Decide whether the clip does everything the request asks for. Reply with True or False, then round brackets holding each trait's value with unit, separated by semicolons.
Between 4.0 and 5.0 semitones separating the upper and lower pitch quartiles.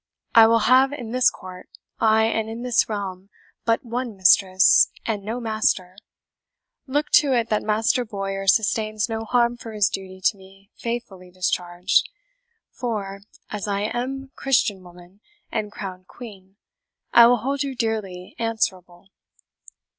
False (3.6 semitones)